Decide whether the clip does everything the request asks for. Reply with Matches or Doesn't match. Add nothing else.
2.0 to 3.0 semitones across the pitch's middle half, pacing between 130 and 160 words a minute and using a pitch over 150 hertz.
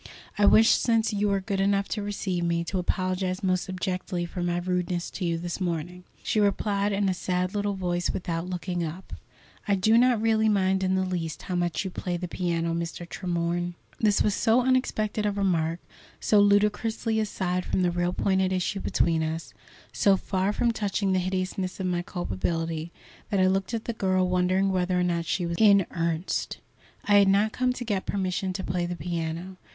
Doesn't match